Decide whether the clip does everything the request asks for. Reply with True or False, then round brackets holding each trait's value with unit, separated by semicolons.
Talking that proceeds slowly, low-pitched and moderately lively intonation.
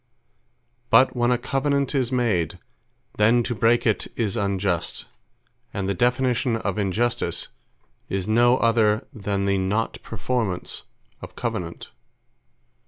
True (120 wpm; 115 Hz; 3.6 semitones)